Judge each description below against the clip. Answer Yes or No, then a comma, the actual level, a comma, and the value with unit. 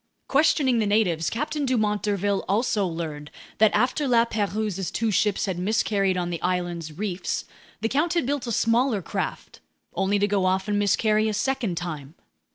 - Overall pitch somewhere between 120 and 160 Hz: No, high, 205 Hz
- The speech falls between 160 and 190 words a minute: Yes, average, 170 wpm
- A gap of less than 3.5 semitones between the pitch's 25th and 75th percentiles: No, average, 3.8 semitones